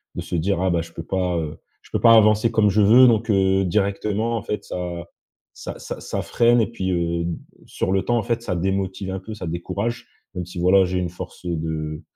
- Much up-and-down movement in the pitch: No, average, 3.6 semitones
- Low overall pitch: Yes, very low, 95 Hz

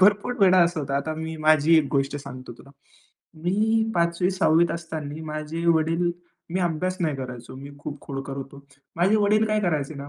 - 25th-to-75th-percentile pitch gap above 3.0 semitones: Yes, average, 4.0 semitones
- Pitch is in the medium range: Yes, medium, 160 Hz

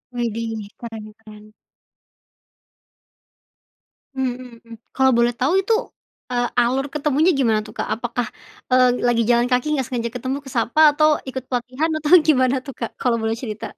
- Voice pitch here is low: No, high, 245 Hz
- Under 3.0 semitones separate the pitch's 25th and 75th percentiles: Yes, narrow, 2.4 semitones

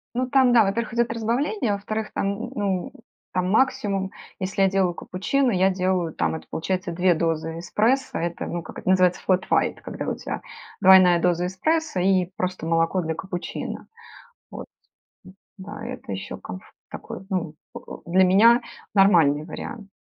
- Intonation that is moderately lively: Yes, average, 3.6 semitones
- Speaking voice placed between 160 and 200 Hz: Yes, high, 190 Hz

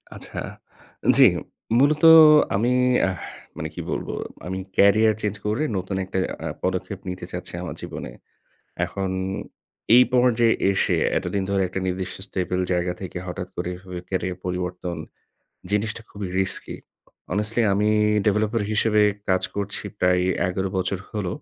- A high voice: No, very low, 95 Hz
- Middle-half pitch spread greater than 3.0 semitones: No, average, 2.7 semitones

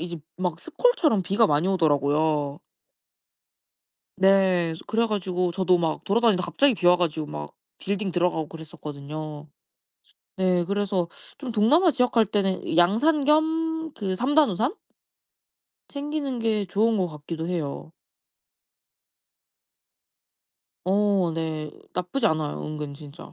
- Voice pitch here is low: No, medium, 185 Hz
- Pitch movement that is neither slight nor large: No, wide, 5.8 semitones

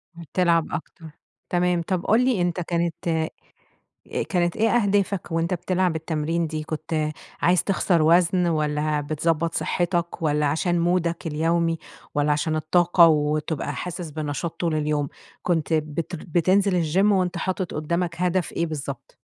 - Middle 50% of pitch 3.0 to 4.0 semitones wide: No, narrow, 2.4 semitones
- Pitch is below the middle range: No, medium, 170 Hz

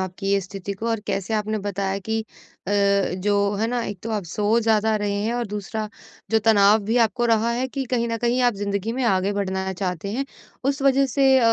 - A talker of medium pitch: No, high, 215 Hz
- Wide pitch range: No, average, 2.8 semitones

